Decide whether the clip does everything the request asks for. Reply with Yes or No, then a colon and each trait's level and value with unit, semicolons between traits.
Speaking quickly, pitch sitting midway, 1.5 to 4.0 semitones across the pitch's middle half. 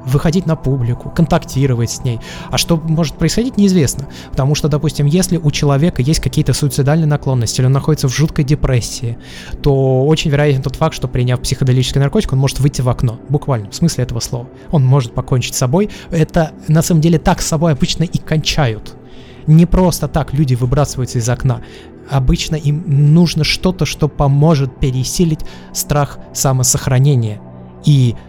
Yes: fast, 165 wpm; medium, 145 Hz; average, 3.7 semitones